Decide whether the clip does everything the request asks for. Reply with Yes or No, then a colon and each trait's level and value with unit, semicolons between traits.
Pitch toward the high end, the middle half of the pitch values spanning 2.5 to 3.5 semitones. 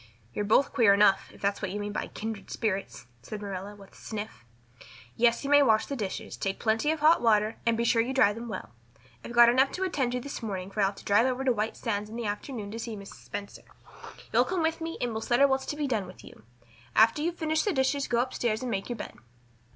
No: high, 230 Hz; average, 4.4 semitones